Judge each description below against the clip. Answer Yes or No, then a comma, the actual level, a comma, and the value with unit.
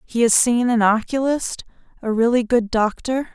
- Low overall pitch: No, high, 235 Hz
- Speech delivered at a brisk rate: No, average, 145 wpm